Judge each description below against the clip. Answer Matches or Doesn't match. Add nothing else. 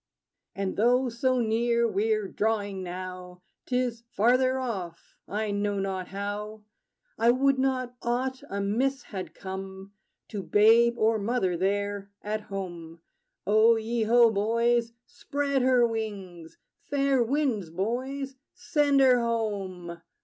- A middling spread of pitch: Matches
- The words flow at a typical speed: Doesn't match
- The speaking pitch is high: Matches